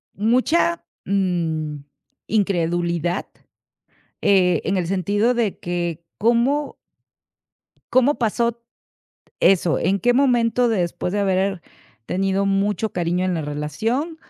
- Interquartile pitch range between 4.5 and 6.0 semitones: Yes, average, 5.0 semitones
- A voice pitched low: No, high, 195 Hz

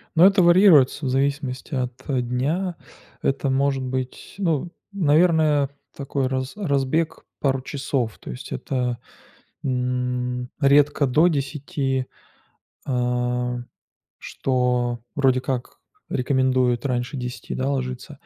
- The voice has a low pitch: Yes, low, 130 Hz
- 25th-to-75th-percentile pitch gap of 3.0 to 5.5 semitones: No, narrow, 2.5 semitones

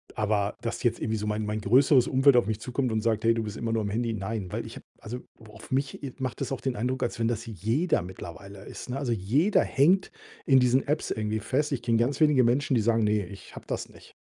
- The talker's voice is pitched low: Yes, low, 115 Hz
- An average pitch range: Yes, average, 3.7 semitones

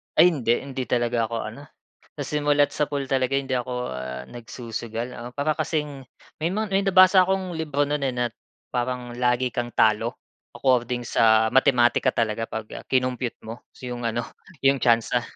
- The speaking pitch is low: Yes, low, 125 Hz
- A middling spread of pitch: Yes, average, 3.4 semitones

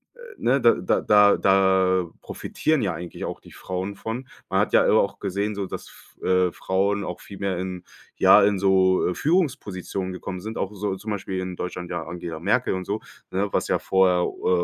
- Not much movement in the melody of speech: Yes, narrow, 1.9 semitones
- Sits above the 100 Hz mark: No, very low, 95 Hz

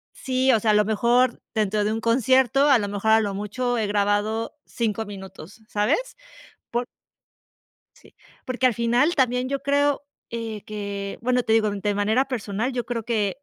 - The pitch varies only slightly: No, average, 3.3 semitones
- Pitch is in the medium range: No, high, 225 Hz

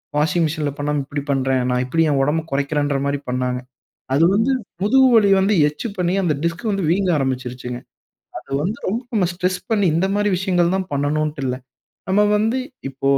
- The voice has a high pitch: No, medium, 160 Hz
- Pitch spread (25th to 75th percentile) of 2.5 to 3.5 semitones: No, average, 5.3 semitones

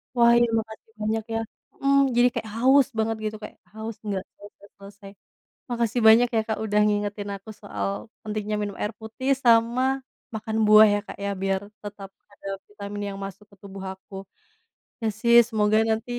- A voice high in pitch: Yes, high, 215 Hz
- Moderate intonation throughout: No, narrow, 1.9 semitones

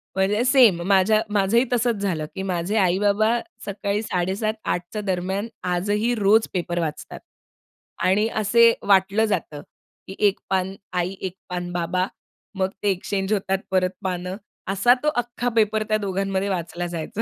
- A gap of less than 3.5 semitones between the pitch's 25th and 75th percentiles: Yes, average, 2.8 semitones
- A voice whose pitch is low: No, high, 195 Hz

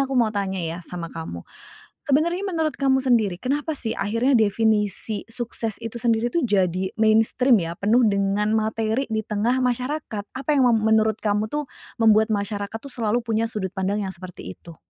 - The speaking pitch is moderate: No, high, 220 Hz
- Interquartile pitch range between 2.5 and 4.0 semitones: Yes, average, 3.5 semitones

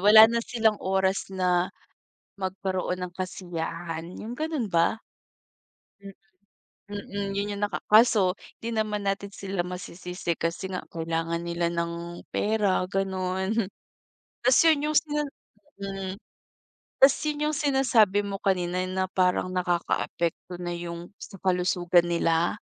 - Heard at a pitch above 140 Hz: Yes, high, 190 Hz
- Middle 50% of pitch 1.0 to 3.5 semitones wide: Yes, average, 3.0 semitones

